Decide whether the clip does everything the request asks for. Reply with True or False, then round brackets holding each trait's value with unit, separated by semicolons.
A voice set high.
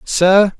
True (195 Hz)